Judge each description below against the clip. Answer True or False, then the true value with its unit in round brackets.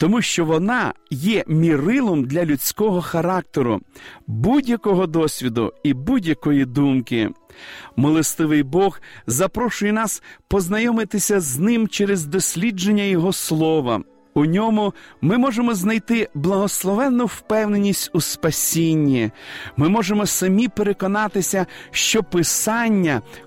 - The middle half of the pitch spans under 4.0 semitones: False (5.4 semitones)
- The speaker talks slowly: True (100 wpm)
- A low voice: False (190 Hz)